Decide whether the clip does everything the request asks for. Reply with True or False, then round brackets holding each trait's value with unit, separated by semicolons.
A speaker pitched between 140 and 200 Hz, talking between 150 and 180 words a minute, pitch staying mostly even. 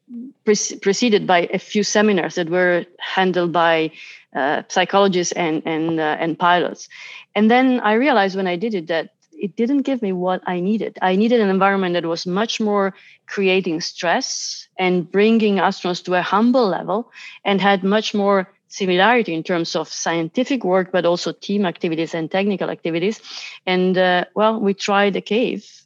False (190 Hz; 170 wpm; 3.1 semitones)